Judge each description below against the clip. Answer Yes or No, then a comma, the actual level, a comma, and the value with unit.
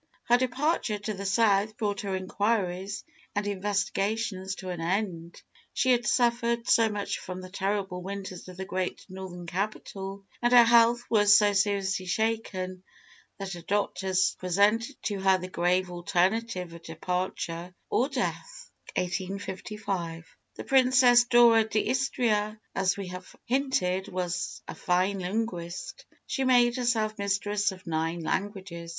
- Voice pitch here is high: Yes, high, 200 Hz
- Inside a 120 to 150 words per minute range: Yes, average, 140 wpm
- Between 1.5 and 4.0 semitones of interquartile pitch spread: Yes, average, 3.5 semitones